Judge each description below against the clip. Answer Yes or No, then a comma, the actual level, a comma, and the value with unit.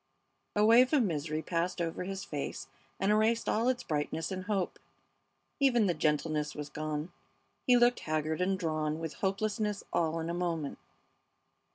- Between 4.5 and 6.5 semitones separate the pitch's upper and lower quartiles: Yes, average, 5.2 semitones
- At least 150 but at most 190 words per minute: Yes, average, 160 wpm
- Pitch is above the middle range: No, medium, 175 Hz